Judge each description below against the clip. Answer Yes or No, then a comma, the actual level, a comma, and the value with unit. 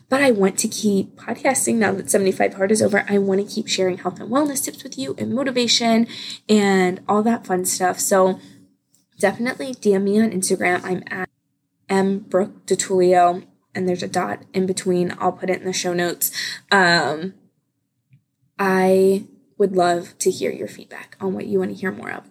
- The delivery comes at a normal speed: Yes, average, 185 wpm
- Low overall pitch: No, high, 190 Hz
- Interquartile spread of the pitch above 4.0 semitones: No, average, 2.7 semitones